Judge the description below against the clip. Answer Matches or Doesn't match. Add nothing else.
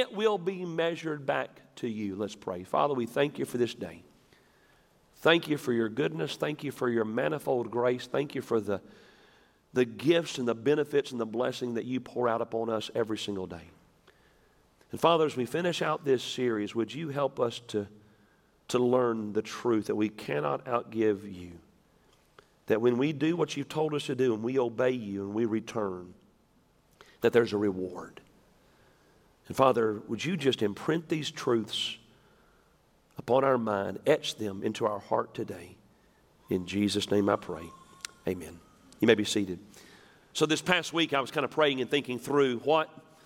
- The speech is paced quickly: Doesn't match